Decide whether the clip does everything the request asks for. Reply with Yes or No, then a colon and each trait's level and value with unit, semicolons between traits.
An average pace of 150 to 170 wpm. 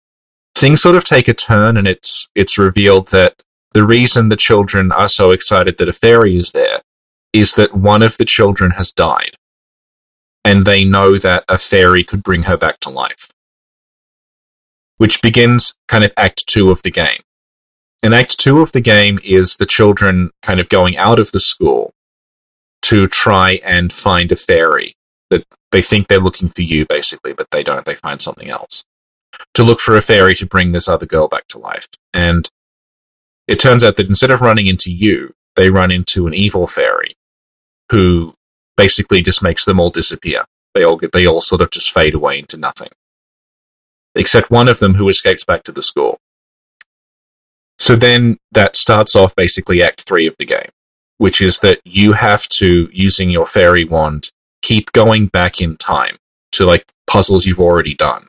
No: average, 185 wpm